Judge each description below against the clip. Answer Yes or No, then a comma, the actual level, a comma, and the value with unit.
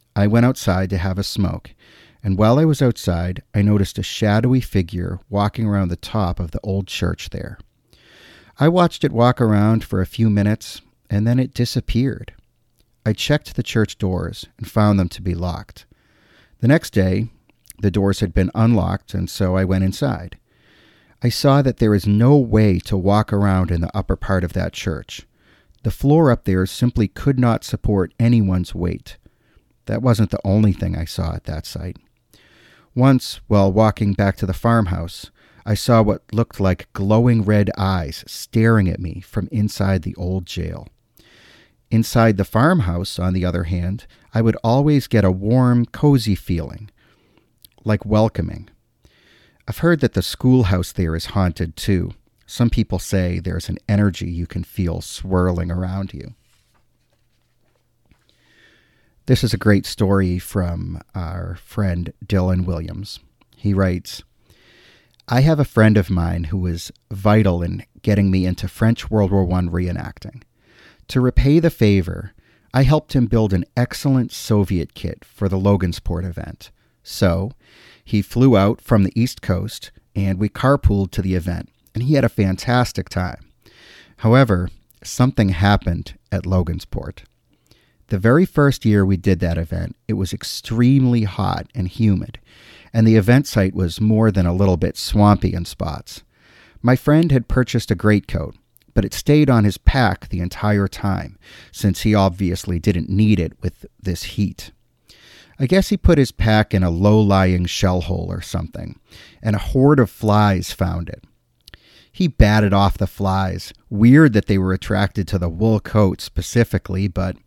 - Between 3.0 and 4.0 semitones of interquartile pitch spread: Yes, average, 3.7 semitones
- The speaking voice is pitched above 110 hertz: No, low, 100 Hz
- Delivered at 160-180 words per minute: Yes, average, 165 wpm